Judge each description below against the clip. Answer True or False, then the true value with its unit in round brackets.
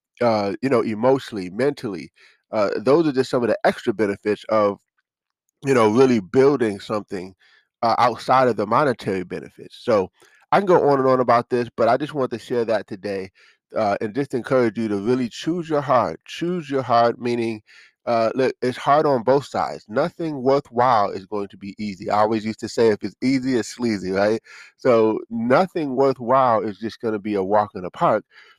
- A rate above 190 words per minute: True (200 wpm)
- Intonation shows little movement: False (3.8 semitones)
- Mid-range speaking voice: False (115 Hz)